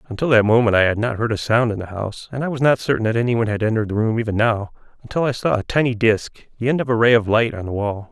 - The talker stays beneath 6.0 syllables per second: No, 6.9 syllables/s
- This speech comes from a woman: No, male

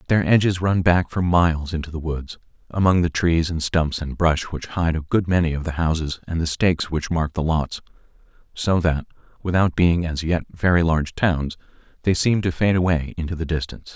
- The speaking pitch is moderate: No, very low, 85 Hz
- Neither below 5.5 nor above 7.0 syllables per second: No, 5.3 syllables/s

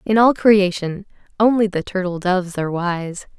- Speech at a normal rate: Yes, average, 160 wpm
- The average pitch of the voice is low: No, high, 190 Hz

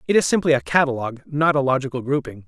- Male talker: Yes, male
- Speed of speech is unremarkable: No, fast, 220 wpm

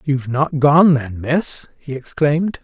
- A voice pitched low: No, medium, 145 Hz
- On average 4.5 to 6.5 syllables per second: No, 4.1 syllables/s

